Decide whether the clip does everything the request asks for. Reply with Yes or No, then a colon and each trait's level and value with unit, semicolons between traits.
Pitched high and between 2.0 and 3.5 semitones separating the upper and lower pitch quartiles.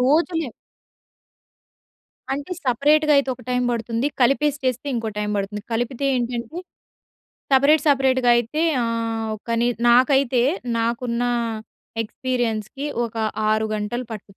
Yes: high, 245 Hz; average, 3.2 semitones